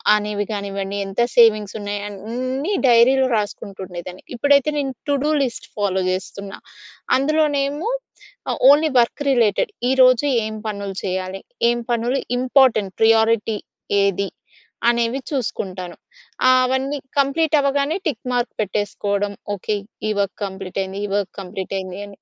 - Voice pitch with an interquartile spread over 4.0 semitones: Yes, average, 5.0 semitones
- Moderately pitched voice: No, high, 220 Hz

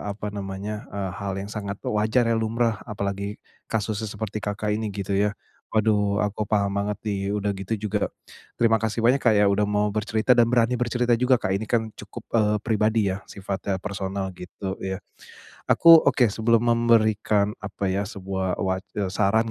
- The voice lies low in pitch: Yes, low, 105 Hz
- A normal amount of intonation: No, narrow, 1.9 semitones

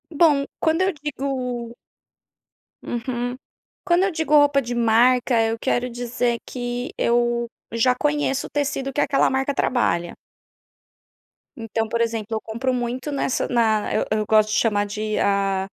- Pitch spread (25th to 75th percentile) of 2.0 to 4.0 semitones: Yes, average, 3.3 semitones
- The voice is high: Yes, high, 245 Hz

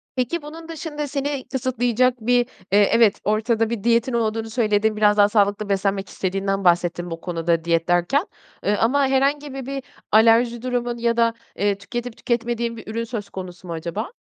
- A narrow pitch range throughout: No, average, 3.8 semitones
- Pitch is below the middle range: No, high, 225 Hz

